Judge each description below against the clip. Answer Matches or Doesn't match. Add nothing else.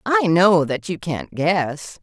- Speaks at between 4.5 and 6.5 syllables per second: Doesn't match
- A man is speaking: Doesn't match